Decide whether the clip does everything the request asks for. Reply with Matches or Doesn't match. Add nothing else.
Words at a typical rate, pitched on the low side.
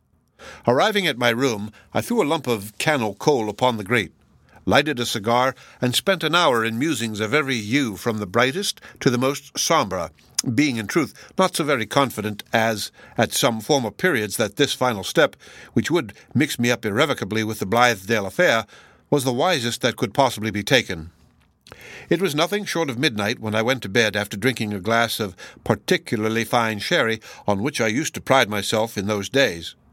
Matches